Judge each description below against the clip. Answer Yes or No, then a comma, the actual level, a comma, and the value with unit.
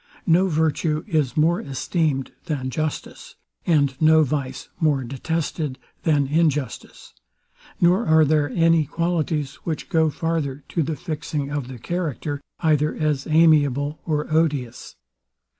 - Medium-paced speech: No, slow, 125 wpm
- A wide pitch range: No, narrow, 2.4 semitones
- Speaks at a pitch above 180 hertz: No, medium, 155 Hz